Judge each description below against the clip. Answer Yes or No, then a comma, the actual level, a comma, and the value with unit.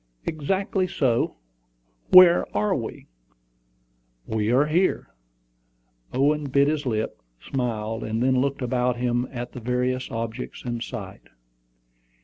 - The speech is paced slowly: Yes, slow, 120 wpm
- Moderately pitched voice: No, low, 125 Hz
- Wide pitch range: No, average, 3.3 semitones